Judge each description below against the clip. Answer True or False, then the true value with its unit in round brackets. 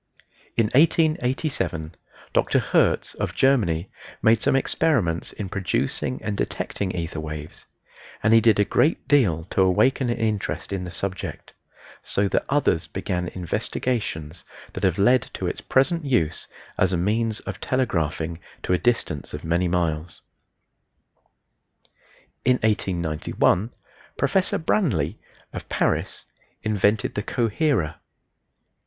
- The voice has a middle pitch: False (100 Hz)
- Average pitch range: False (6.5 semitones)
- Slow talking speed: True (125 wpm)